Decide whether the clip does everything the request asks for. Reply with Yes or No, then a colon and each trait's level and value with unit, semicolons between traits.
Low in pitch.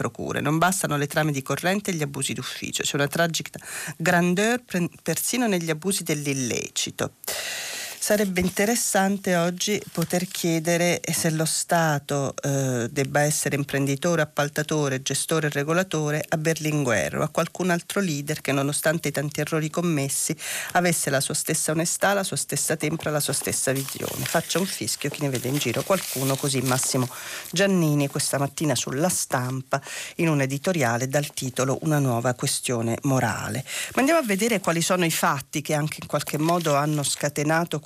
No: medium, 155 Hz